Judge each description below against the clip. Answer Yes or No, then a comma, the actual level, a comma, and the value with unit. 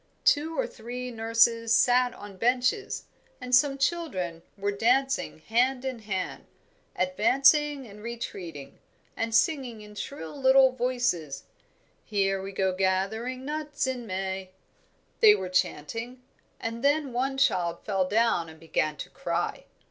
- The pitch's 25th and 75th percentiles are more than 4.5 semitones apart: Yes, wide, 5.5 semitones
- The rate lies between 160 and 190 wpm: No, slow, 135 wpm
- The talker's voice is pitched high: Yes, high, 230 Hz